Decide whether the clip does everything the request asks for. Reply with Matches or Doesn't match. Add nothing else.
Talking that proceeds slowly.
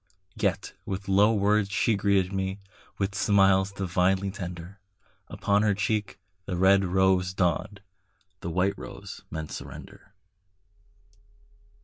Matches